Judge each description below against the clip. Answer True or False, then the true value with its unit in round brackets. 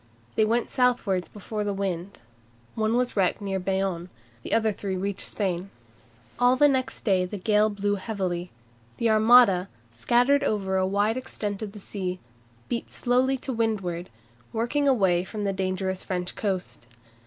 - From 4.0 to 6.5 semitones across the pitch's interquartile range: False (3.5 semitones)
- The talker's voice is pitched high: True (205 Hz)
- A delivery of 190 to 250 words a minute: False (150 wpm)